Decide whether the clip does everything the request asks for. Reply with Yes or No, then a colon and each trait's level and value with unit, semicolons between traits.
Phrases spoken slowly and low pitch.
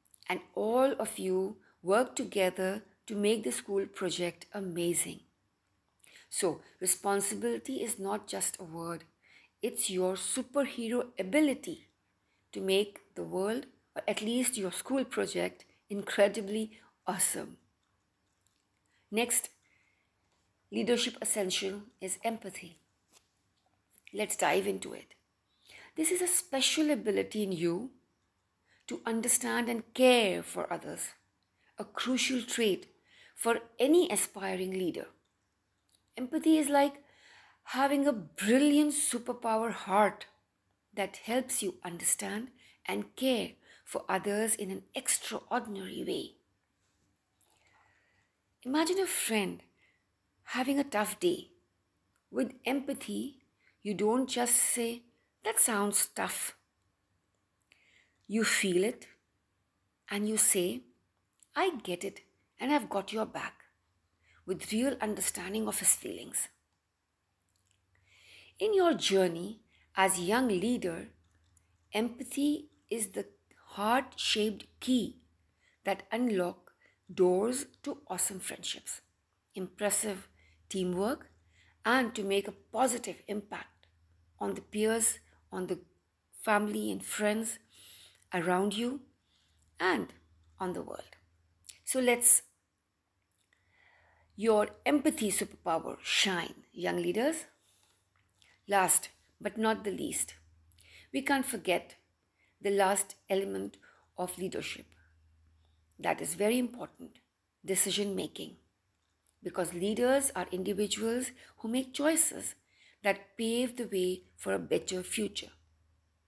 No: slow, 105 wpm; high, 200 Hz